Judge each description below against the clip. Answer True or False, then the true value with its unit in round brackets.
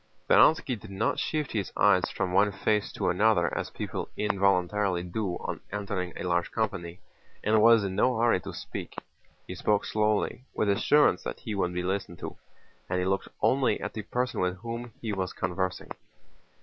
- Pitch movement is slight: False (3.3 semitones)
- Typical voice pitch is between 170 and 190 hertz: False (100 Hz)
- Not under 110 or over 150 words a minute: False (180 wpm)